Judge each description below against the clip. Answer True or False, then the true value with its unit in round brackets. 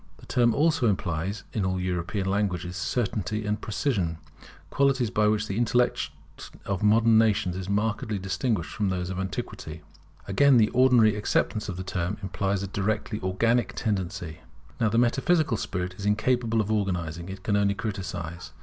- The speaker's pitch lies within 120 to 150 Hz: False (100 Hz)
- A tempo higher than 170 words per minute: False (160 wpm)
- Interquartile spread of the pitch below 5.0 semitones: True (3.3 semitones)